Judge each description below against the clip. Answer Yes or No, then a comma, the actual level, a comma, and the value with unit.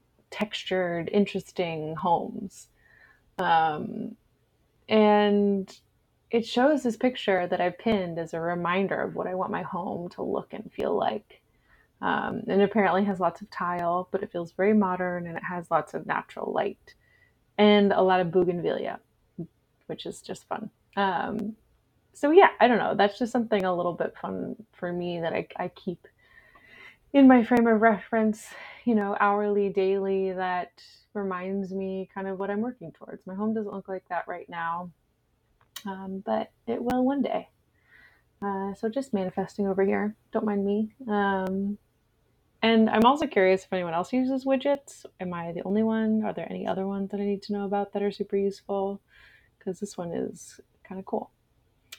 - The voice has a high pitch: Yes, high, 200 Hz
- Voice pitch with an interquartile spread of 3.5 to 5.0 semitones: No, average, 2.9 semitones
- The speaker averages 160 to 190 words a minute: Yes, average, 175 wpm